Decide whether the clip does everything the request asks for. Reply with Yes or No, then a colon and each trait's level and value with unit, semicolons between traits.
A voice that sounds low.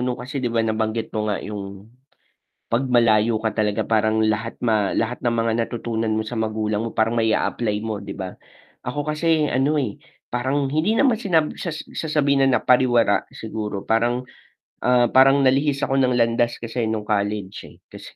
Yes: low, 115 Hz